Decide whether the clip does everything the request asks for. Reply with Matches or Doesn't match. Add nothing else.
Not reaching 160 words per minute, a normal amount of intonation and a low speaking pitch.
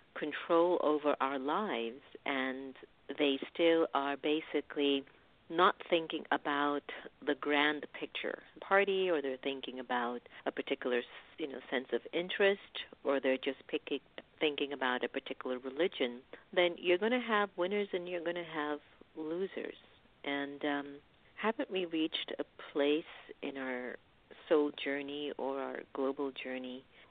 Doesn't match